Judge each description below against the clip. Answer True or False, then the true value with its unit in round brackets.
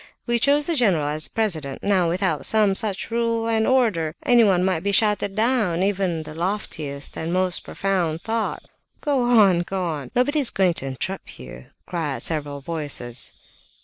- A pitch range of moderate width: False (5.7 semitones)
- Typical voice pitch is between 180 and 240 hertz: True (190 Hz)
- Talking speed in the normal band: True (170 wpm)